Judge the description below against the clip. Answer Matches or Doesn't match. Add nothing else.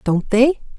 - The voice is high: Matches